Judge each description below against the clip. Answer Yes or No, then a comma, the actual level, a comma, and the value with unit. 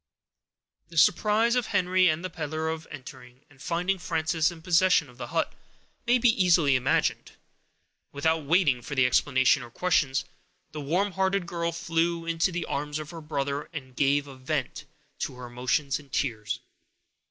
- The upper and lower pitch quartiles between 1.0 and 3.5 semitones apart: No, average, 4.1 semitones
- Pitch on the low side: No, medium, 160 Hz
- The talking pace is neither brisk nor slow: Yes, average, 165 wpm